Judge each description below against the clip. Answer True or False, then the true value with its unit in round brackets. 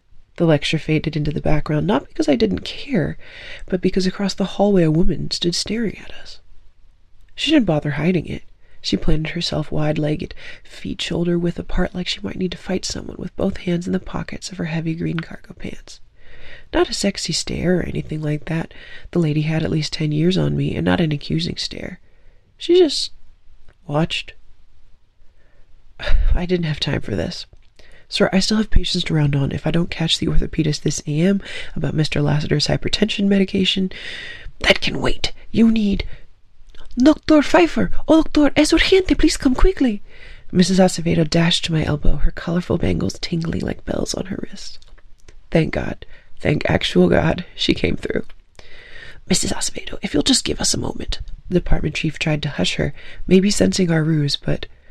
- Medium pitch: True (175 Hz)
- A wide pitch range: False (4.9 semitones)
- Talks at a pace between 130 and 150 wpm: False (180 wpm)